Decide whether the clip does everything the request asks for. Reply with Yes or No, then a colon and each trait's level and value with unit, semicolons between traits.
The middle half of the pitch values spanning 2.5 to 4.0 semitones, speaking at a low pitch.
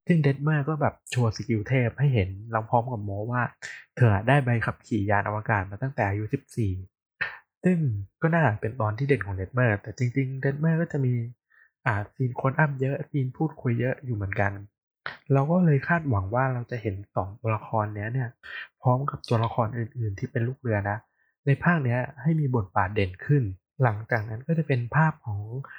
No: average, 4.4 semitones; low, 120 Hz